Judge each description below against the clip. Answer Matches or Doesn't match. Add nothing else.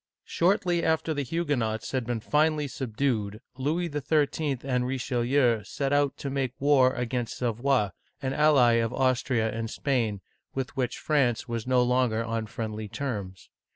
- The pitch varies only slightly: Doesn't match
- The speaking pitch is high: Doesn't match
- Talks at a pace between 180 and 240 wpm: Doesn't match